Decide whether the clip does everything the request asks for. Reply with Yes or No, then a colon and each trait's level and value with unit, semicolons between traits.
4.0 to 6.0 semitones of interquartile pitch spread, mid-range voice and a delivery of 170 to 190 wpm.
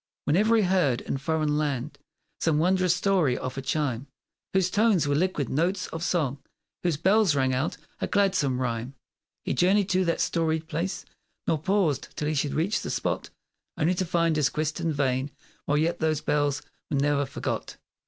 Yes: average, 4.3 semitones; medium, 155 Hz; average, 180 wpm